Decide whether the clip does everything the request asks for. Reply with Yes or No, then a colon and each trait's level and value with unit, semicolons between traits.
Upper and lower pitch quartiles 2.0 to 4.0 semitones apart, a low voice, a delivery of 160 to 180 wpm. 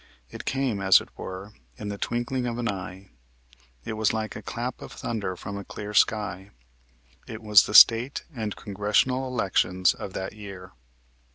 Yes: average, 2.9 semitones; low, 105 Hz; average, 170 wpm